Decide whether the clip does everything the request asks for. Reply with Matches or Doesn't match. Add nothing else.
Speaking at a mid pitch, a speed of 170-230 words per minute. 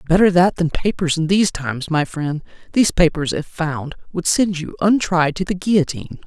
Matches